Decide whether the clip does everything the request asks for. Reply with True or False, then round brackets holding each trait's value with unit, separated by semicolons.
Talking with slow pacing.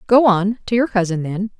False (225 wpm)